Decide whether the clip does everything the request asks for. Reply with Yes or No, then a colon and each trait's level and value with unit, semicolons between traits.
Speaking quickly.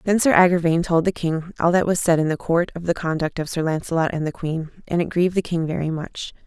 Yes: fast, 270 wpm